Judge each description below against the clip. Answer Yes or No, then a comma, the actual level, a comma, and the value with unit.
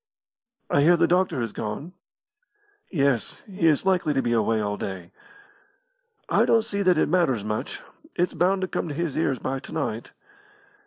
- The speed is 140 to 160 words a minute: No, average, 175 wpm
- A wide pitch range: Yes, wide, 7.4 semitones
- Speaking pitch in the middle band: Yes, medium, 150 Hz